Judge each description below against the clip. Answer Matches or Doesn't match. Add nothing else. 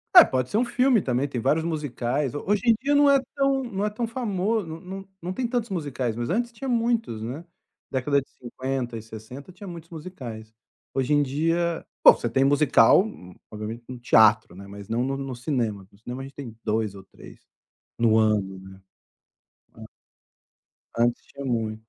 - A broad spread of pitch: Matches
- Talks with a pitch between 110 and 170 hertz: Matches